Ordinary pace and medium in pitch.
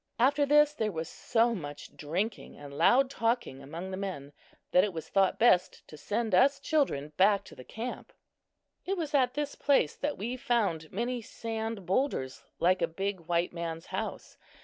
No: average, 175 wpm; high, 210 Hz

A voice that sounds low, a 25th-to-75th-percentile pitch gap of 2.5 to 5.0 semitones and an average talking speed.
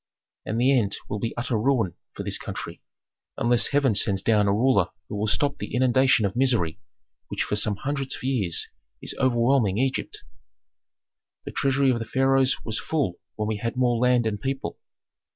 Yes: low, 120 Hz; average, 3.9 semitones; average, 180 wpm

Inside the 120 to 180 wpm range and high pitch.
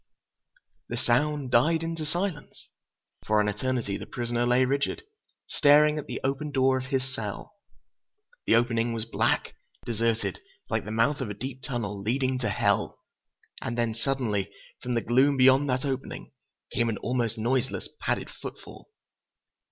No: average, 150 wpm; low, 125 Hz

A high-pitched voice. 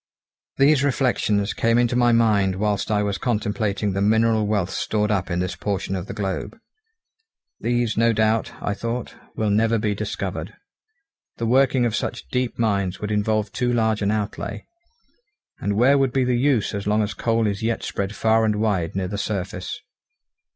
No: low, 110 Hz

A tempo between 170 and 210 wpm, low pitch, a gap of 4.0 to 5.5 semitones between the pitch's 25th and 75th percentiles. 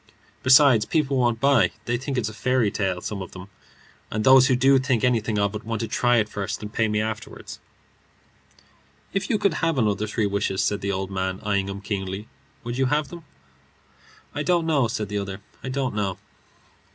Yes: average, 200 wpm; low, 110 Hz; average, 4.4 semitones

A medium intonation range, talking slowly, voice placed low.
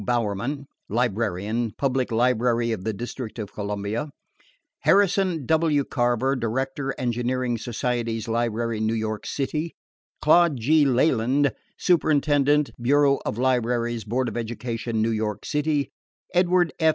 Yes: average, 4.0 semitones; slow, 120 wpm; low, 120 Hz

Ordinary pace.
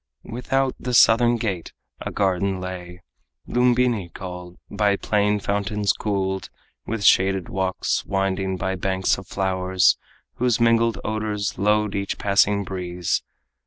No: slow, 125 wpm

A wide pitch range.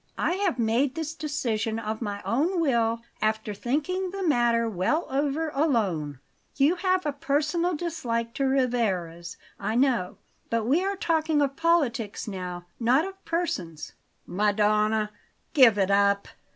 Yes: wide, 6.6 semitones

